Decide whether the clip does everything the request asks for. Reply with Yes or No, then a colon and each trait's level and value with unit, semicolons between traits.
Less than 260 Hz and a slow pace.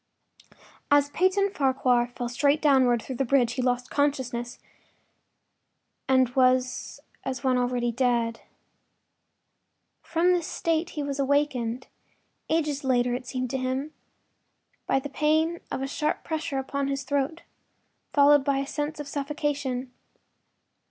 No: very high, 270 Hz; slow, 130 wpm